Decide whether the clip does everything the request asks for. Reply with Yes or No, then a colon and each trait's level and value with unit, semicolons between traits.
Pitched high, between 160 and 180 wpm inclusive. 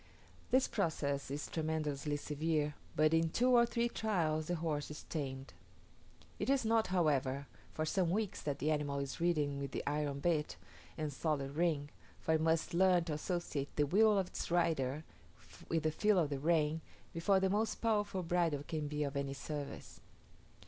No: medium, 155 Hz; average, 175 wpm